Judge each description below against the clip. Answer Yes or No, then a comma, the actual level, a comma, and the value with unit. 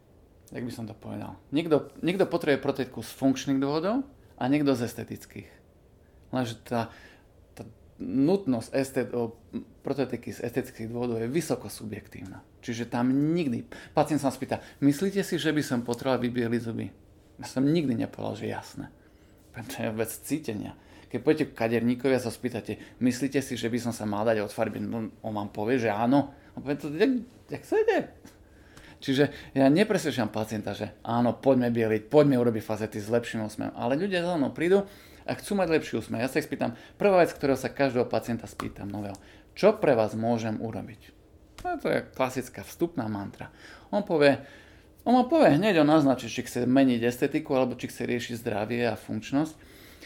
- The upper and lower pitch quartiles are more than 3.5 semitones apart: Yes, average, 4.2 semitones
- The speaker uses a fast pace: Yes, fast, 175 wpm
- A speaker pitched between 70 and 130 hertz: Yes, low, 120 Hz